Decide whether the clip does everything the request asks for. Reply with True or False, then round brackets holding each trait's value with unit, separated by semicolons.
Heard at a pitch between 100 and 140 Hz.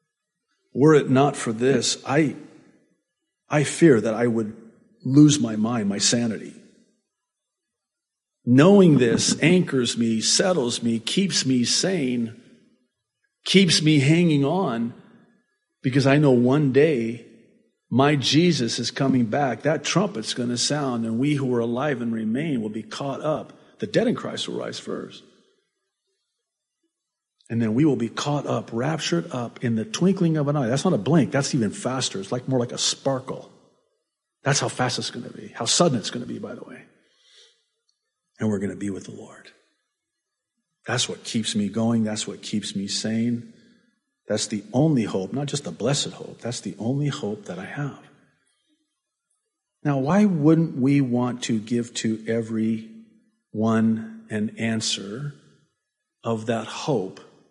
True (135 Hz)